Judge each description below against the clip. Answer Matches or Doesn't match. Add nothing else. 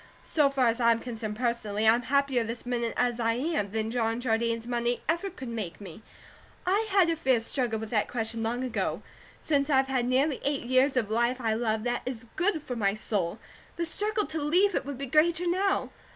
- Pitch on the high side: Matches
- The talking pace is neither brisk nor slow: Doesn't match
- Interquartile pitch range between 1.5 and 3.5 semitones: Doesn't match